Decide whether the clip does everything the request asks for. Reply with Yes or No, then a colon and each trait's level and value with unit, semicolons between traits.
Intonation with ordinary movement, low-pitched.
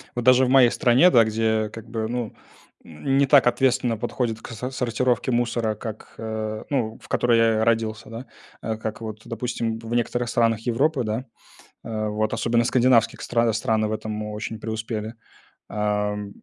No: narrow, 1.9 semitones; low, 115 Hz